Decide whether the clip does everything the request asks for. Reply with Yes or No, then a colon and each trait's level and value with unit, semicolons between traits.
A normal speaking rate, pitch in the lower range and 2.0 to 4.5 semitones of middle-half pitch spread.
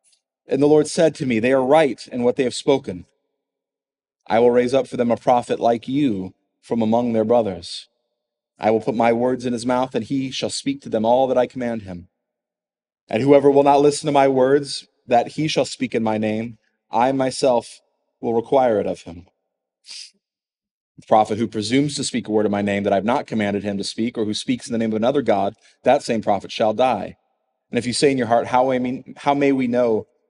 No: fast, 225 wpm; low, 120 Hz; average, 3.7 semitones